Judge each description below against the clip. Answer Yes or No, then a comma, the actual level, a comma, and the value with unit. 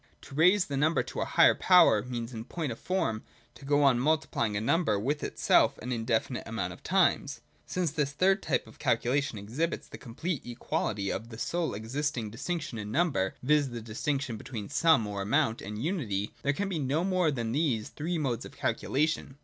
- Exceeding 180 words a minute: Yes, average, 200 wpm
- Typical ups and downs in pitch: No, wide, 5.7 semitones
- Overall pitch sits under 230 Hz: Yes, low, 135 Hz